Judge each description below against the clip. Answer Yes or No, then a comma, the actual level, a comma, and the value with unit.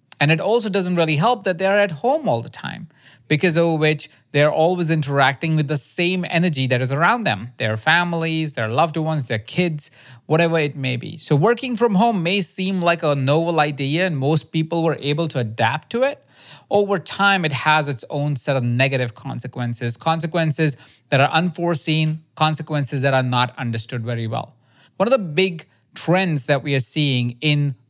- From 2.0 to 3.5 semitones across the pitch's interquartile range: No, average, 4.2 semitones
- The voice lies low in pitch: No, medium, 155 Hz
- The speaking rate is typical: Yes, average, 190 wpm